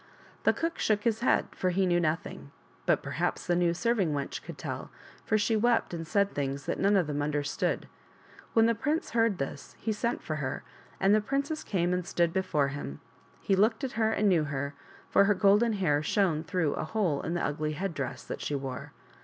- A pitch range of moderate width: No, wide, 6.3 semitones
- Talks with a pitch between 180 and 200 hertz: Yes, medium, 185 Hz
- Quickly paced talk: Yes, fast, 210 wpm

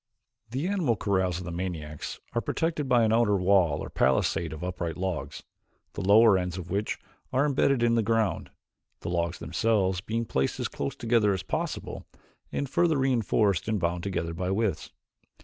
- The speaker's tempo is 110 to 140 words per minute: No, average, 175 wpm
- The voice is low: Yes, low, 100 Hz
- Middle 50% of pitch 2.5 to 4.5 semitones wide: No, average, 4.9 semitones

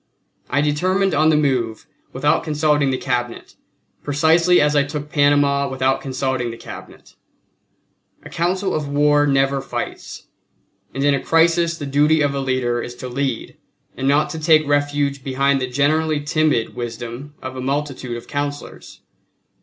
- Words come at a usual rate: Yes, average, 155 wpm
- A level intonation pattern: Yes, narrow, 2.3 semitones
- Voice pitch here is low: No, medium, 145 Hz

